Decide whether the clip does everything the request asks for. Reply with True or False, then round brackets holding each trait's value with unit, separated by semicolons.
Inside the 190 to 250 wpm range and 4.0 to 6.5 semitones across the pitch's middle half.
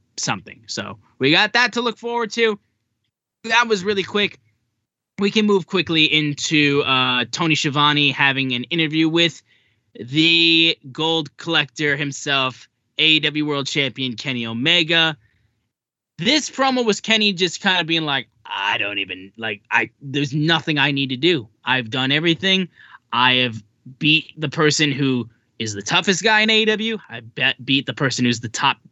False (160 wpm; 5.6 semitones)